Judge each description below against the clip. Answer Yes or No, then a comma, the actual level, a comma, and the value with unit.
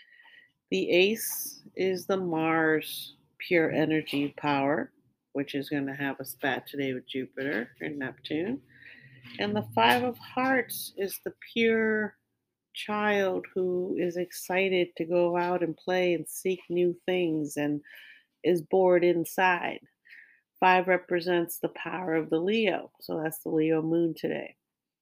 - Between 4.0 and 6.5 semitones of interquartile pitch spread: No, average, 3.4 semitones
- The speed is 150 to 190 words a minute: No, average, 140 wpm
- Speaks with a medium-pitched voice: Yes, medium, 175 Hz